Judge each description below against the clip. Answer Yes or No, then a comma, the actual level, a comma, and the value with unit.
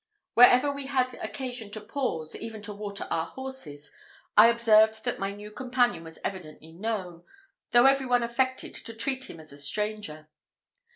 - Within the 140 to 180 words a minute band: Yes, average, 165 wpm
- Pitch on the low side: No, high, 220 Hz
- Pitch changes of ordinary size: Yes, average, 4.8 semitones